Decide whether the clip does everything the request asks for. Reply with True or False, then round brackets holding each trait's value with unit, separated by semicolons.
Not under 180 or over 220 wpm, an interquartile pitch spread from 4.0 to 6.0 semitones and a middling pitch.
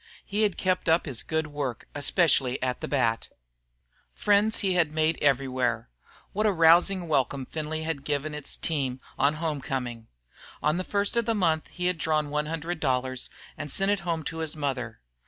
True (190 wpm; 4.3 semitones; 155 Hz)